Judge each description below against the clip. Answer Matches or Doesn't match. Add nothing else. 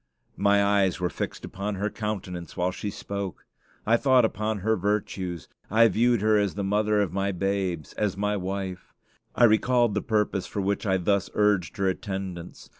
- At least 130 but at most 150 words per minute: Doesn't match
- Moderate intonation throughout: Doesn't match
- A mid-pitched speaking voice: Doesn't match